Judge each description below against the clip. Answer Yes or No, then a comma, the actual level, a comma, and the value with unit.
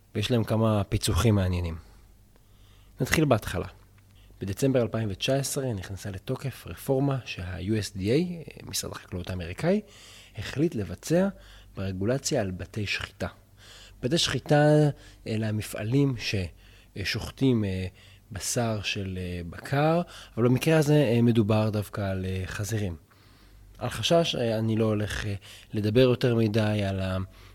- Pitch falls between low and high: No, low, 105 Hz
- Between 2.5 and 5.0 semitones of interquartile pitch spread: Yes, average, 4.2 semitones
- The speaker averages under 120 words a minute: Yes, slow, 100 wpm